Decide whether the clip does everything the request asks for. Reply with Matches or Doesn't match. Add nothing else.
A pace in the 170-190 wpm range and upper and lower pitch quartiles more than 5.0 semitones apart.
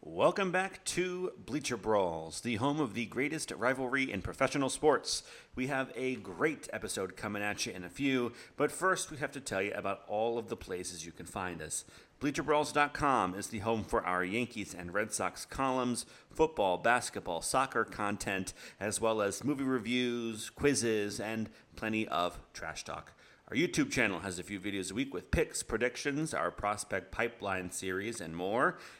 Matches